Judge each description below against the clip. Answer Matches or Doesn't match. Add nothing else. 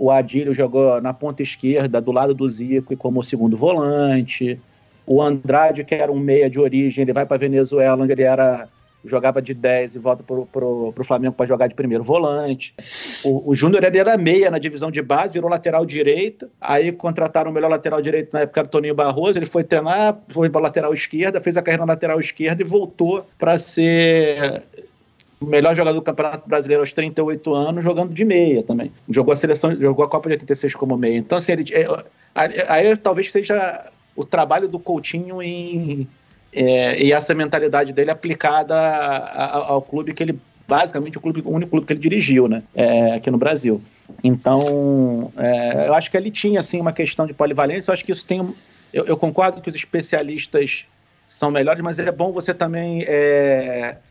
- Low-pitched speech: Doesn't match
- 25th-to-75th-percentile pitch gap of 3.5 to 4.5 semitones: Matches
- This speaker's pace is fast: Matches